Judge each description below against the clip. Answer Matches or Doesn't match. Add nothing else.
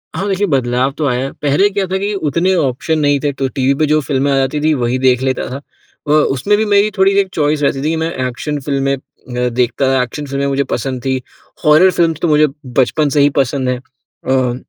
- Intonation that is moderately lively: Matches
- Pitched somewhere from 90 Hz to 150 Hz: Matches